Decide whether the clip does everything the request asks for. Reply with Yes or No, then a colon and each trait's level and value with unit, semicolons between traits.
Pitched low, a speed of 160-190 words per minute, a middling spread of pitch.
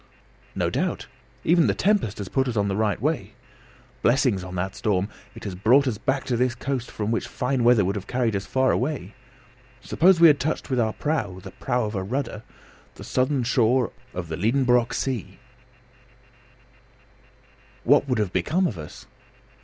Yes: low, 120 Hz; average, 180 wpm; average, 4.7 semitones